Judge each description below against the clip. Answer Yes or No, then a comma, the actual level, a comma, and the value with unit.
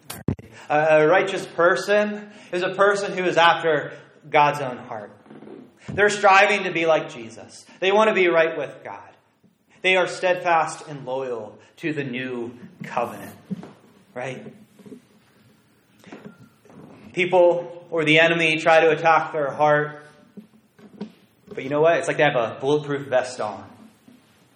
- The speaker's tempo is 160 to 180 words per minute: No, slow, 135 wpm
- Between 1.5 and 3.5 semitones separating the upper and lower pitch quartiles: No, average, 4.3 semitones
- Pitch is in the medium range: Yes, medium, 165 Hz